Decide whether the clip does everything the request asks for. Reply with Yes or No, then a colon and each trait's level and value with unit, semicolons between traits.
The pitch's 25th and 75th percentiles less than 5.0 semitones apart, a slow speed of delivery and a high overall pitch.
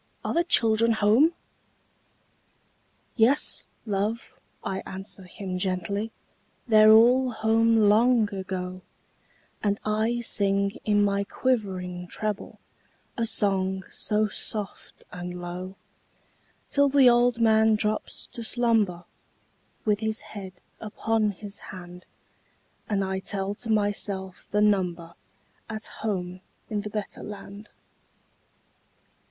Yes: average, 2.7 semitones; slow, 110 wpm; high, 210 Hz